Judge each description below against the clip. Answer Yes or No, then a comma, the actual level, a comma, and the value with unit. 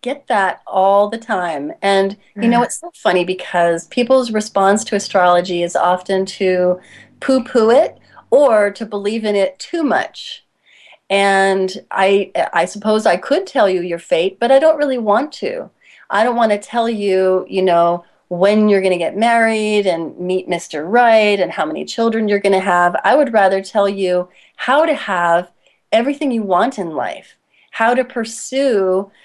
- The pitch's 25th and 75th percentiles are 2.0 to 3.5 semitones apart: No, average, 4.0 semitones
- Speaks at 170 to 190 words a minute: Yes, average, 175 wpm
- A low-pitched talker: No, high, 200 Hz